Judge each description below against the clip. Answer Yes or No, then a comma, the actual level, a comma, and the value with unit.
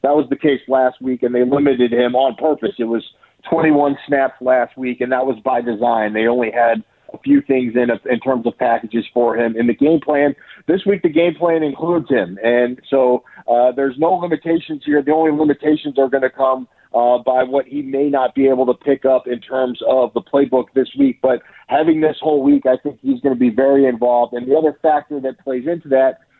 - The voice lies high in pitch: No, low, 135 Hz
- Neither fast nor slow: No, fast, 230 wpm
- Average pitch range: Yes, average, 3.0 semitones